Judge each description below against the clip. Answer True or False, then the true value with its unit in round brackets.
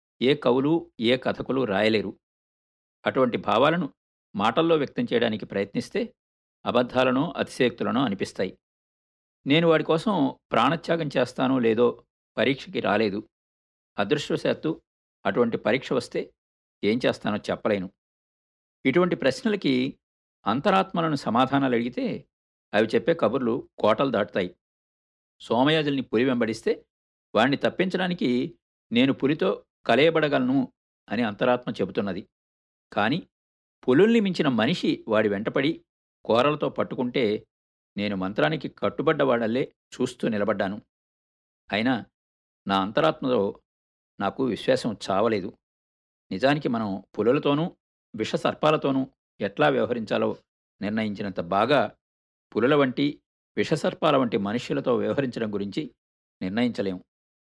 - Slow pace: False (90 wpm)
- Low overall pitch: True (125 Hz)